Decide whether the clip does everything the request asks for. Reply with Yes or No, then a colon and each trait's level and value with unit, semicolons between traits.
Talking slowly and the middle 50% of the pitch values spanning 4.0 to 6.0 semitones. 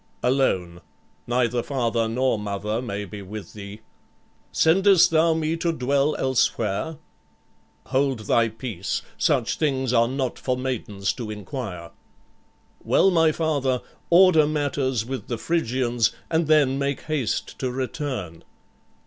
Yes: slow, 125 wpm; average, 5.0 semitones